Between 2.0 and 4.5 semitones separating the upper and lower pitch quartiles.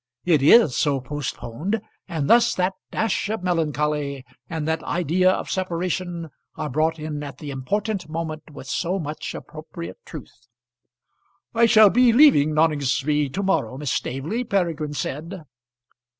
Yes: average, 4.1 semitones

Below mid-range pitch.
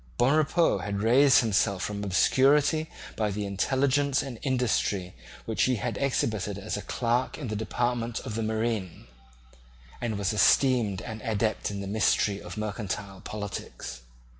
Yes: low, 110 Hz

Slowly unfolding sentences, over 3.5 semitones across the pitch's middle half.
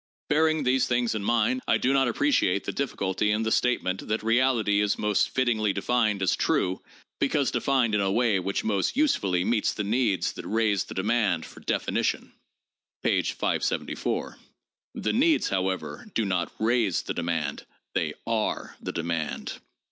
No: average, 160 wpm; average, 4.4 semitones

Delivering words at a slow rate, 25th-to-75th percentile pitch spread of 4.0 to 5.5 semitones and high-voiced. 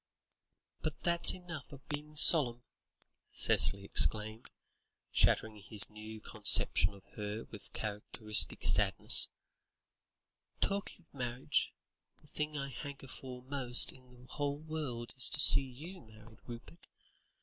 No: slow, 125 wpm; average, 5.2 semitones; low, 125 Hz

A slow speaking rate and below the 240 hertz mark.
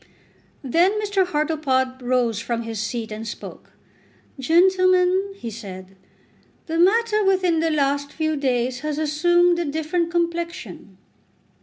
No: slow, 125 wpm; very high, 310 Hz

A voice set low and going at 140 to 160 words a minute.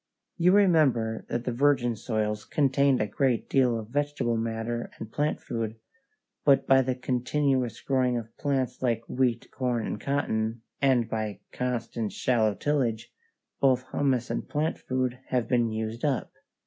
Yes: low, 125 Hz; average, 150 wpm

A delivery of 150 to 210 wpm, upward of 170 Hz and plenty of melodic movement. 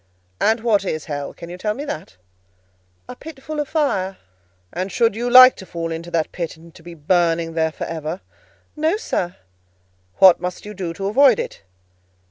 Yes: average, 190 wpm; medium, 185 Hz; wide, 6.3 semitones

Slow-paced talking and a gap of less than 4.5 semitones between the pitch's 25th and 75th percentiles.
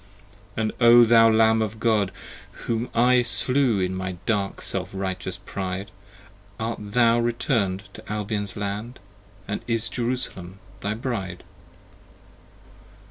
Yes: slow, 125 wpm; average, 2.9 semitones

